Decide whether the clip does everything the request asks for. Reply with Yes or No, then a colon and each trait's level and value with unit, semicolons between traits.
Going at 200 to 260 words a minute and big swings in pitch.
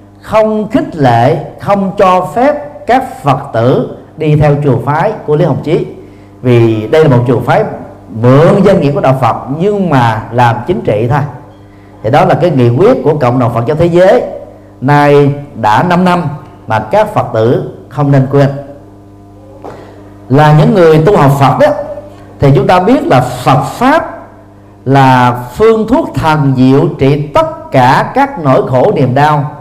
No: average, 175 wpm; wide, 6.5 semitones